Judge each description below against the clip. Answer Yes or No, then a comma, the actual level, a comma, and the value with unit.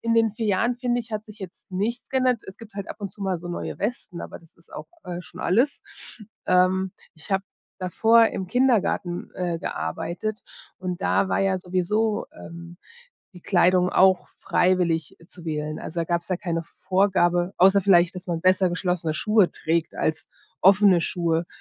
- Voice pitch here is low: No, medium, 185 Hz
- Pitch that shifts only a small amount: No, average, 3.2 semitones